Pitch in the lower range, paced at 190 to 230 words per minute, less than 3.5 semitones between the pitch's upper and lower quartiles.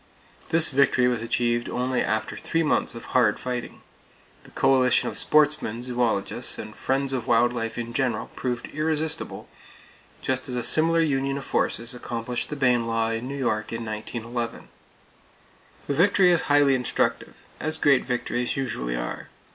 No: low, 125 Hz; average, 155 wpm; average, 3.0 semitones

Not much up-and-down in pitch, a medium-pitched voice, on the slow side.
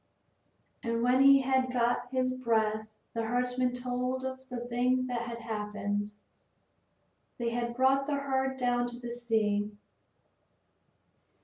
No: narrow, 1.8 semitones; high, 245 Hz; slow, 130 wpm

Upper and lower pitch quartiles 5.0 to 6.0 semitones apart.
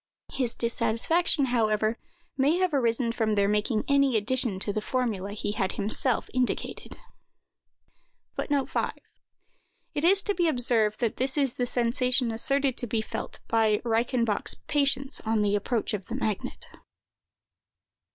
No: average, 3.8 semitones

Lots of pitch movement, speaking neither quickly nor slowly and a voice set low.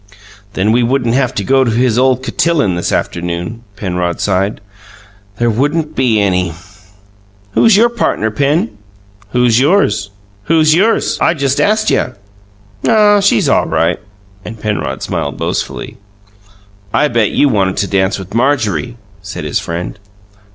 Yes: wide, 6.5 semitones; average, 145 wpm; low, 115 Hz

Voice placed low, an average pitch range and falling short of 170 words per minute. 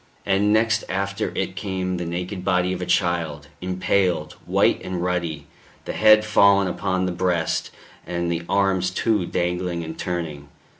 No: very low, 90 Hz; narrow, 2.0 semitones; average, 155 wpm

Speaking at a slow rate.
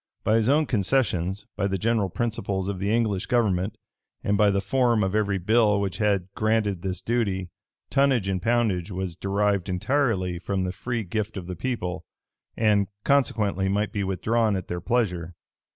No: average, 170 wpm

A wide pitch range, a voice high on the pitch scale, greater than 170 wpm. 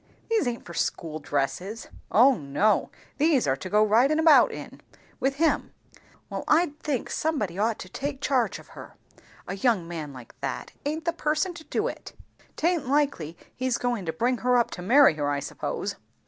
Yes: wide, 8.5 semitones; high, 240 Hz; average, 185 wpm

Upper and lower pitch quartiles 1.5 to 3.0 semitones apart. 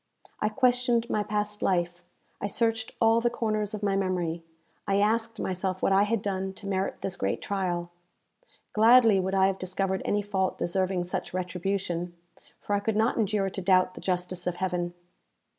Yes: narrow, 2.6 semitones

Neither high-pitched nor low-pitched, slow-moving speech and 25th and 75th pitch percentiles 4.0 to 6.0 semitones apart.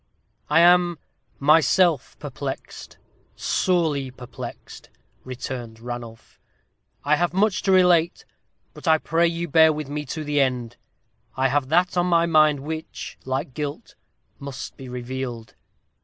Yes: medium, 150 Hz; slow, 130 wpm; average, 4.4 semitones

